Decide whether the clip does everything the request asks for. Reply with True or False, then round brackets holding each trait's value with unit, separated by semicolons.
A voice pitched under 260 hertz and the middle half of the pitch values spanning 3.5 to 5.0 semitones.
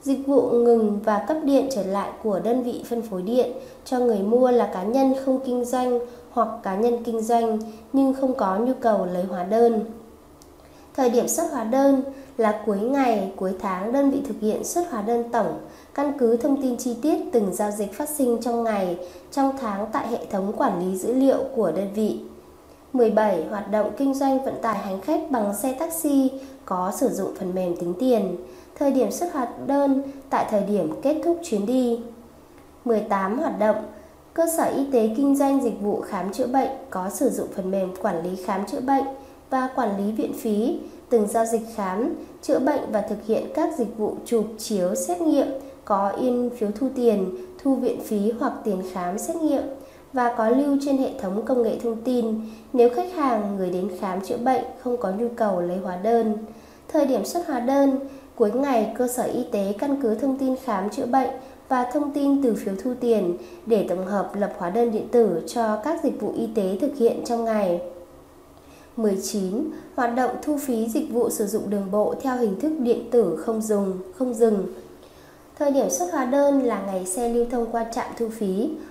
True (235 Hz; 4.3 semitones)